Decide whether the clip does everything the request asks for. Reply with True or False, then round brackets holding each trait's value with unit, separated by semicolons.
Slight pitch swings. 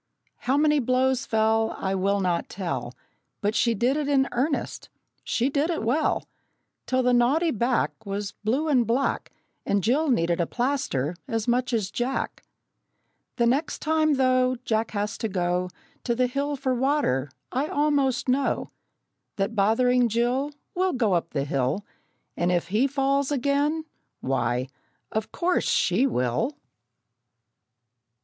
False (5.6 semitones)